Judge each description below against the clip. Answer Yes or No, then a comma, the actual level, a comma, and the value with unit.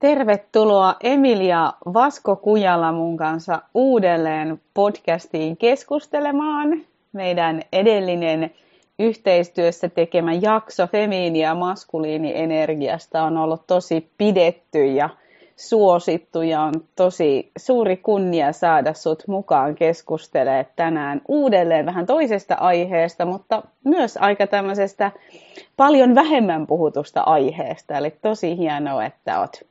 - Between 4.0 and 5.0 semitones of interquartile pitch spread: Yes, average, 4.7 semitones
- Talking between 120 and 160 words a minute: No, average, 105 wpm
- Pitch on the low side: No, medium, 180 Hz